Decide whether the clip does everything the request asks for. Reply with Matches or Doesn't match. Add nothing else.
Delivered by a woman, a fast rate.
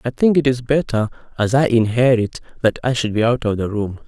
Doesn't match